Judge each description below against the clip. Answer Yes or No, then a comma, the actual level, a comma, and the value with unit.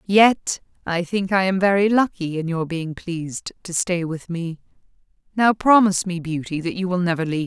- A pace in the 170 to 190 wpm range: No, average, 200 wpm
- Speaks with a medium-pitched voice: Yes, medium, 180 Hz